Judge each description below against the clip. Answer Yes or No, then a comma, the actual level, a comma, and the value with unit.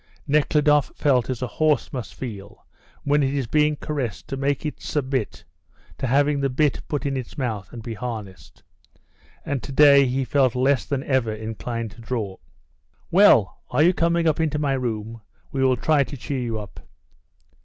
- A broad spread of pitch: No, average, 3.9 semitones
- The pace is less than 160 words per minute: No, average, 175 wpm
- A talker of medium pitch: No, low, 130 Hz